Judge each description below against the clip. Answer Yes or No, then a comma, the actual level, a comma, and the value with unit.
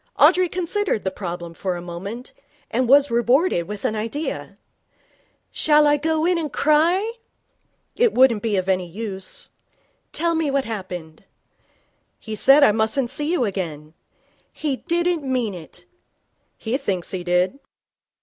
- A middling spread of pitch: No, wide, 8.2 semitones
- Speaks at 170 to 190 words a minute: No, average, 145 wpm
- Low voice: No, high, 235 Hz